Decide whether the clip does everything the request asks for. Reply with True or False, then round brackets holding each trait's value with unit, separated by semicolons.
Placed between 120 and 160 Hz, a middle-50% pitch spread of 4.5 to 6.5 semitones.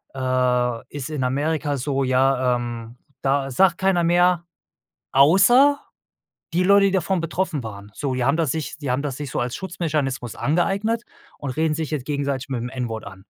True (140 Hz; 5.0 semitones)